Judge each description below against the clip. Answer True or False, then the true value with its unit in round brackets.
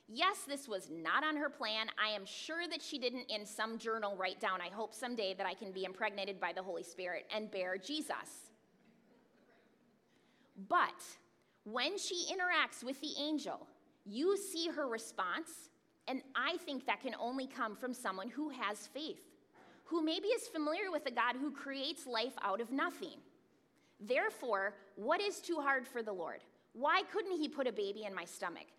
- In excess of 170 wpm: True (180 wpm)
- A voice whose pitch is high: True (255 Hz)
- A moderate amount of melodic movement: False (7.1 semitones)